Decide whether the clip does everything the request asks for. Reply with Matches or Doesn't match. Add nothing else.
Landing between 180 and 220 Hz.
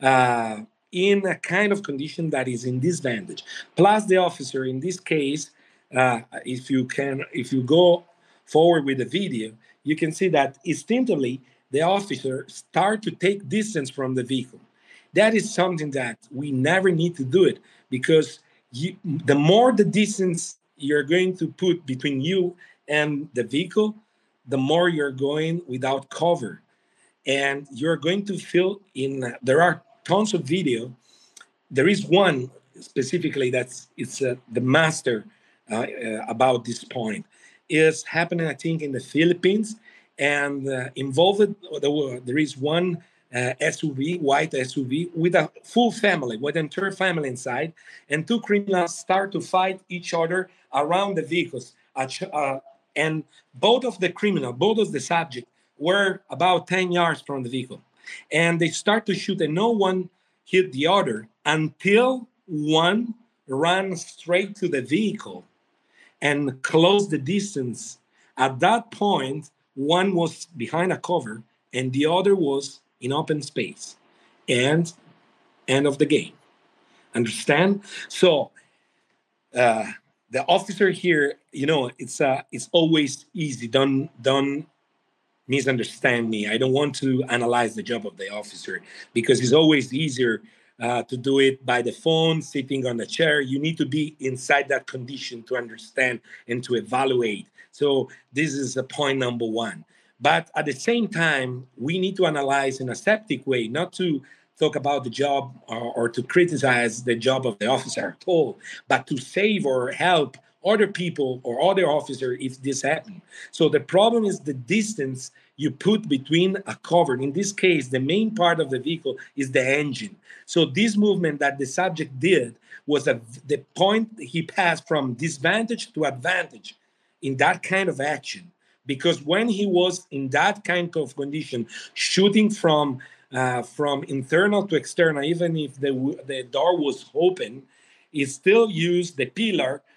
Doesn't match